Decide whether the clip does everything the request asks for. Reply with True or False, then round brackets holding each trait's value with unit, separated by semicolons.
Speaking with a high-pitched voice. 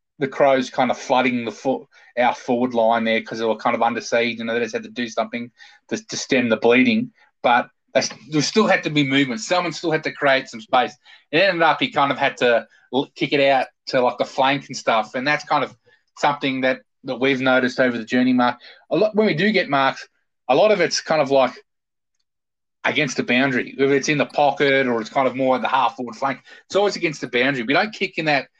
False (135 Hz)